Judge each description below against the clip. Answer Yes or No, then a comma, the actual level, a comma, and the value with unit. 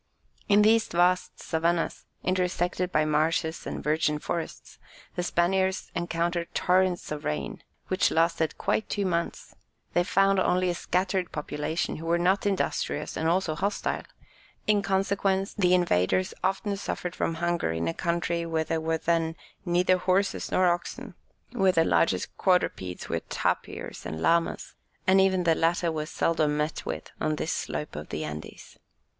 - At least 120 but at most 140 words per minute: No, average, 155 wpm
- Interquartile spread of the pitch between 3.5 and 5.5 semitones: No, narrow, 2.5 semitones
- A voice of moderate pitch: Yes, medium, 175 Hz